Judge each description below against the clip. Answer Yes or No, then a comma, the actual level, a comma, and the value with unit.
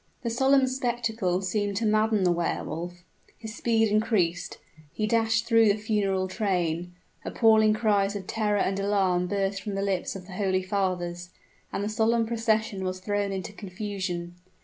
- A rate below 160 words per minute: No, average, 165 wpm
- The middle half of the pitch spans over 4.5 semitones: No, average, 3.0 semitones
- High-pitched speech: Yes, high, 200 Hz